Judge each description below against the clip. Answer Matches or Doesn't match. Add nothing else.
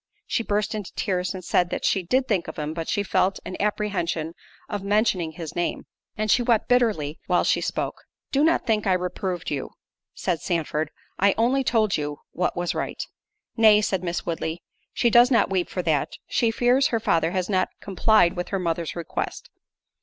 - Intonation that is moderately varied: Matches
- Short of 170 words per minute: Doesn't match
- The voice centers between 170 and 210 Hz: Matches